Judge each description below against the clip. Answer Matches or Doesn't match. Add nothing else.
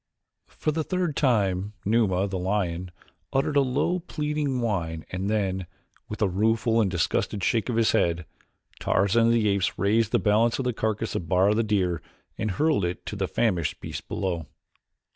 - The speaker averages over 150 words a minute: Matches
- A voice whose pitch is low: Matches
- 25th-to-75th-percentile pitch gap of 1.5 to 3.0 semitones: Doesn't match